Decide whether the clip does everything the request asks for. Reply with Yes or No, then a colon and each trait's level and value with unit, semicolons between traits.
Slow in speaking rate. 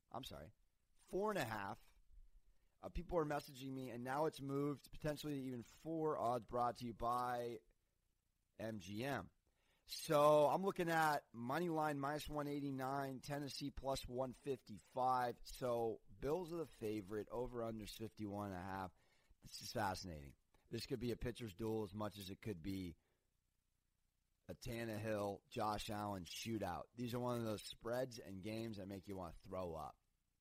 No: average, 170 wpm